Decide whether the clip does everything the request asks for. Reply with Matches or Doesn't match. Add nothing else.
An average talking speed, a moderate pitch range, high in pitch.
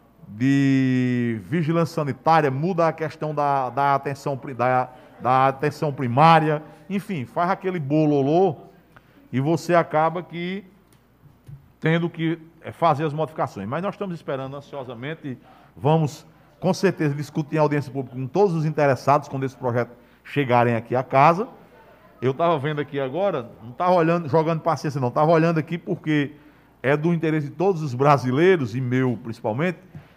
Doesn't match